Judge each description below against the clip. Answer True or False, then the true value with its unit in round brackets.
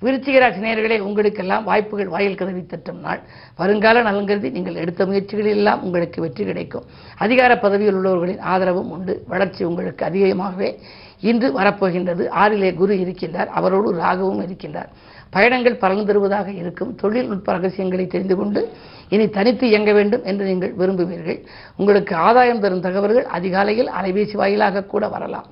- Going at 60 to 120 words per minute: False (130 wpm)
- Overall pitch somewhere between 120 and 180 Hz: False (195 Hz)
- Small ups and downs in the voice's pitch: True (2.3 semitones)